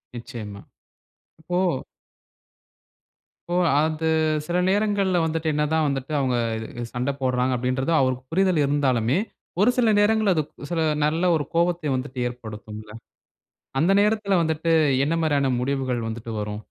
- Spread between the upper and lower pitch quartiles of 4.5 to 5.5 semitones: Yes, average, 5.2 semitones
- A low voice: No, medium, 145 Hz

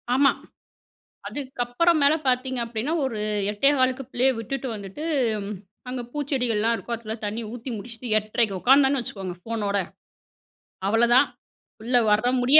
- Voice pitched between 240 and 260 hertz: Yes, high, 245 Hz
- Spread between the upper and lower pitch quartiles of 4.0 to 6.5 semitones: No, average, 3.3 semitones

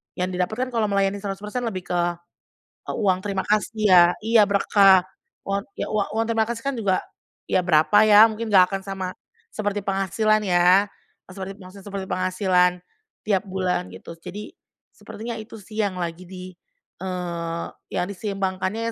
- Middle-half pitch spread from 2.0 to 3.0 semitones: Yes, narrow, 2.6 semitones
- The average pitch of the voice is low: No, high, 195 Hz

